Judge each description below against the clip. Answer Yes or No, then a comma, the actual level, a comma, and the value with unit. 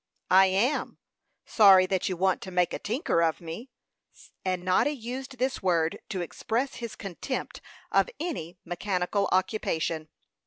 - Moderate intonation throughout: Yes, average, 4.8 semitones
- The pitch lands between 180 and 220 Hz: Yes, high, 190 Hz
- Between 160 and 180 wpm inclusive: No, average, 145 wpm